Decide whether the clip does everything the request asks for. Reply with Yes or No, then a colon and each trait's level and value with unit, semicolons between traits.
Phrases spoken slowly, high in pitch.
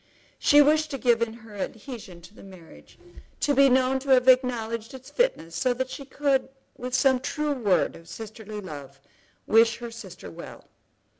No: average, 175 wpm; high, 240 Hz